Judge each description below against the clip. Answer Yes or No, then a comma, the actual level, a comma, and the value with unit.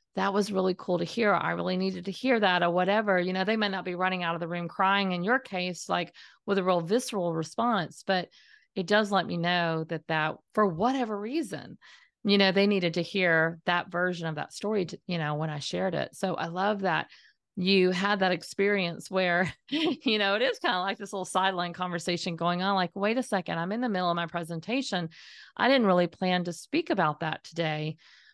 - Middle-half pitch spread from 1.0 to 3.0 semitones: Yes, average, 2.7 semitones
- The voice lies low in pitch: No, medium, 185 Hz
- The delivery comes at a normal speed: No, fast, 225 wpm